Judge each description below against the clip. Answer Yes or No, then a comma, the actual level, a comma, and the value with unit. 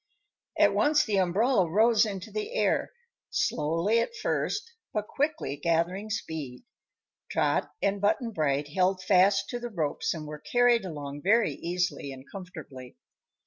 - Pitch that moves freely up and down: Yes, wide, 6.4 semitones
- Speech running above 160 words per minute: No, average, 145 wpm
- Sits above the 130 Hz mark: Yes, high, 190 Hz